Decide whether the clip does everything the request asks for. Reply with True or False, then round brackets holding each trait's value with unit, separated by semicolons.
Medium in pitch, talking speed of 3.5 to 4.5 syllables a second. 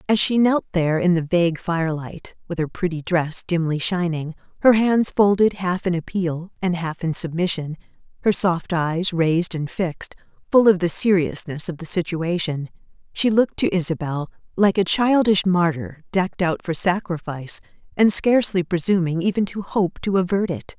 False (175 Hz; 5.0 syllables/s)